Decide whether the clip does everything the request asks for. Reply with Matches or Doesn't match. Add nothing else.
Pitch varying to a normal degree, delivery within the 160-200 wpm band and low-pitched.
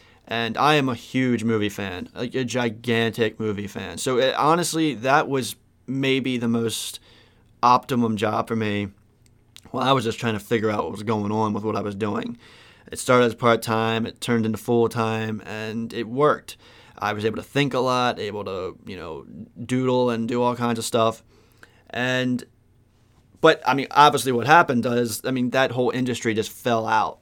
Doesn't match